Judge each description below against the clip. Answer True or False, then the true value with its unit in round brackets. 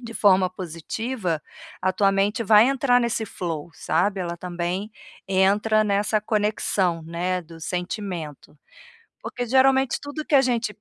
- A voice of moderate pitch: False (200 Hz)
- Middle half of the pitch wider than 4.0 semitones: True (4.4 semitones)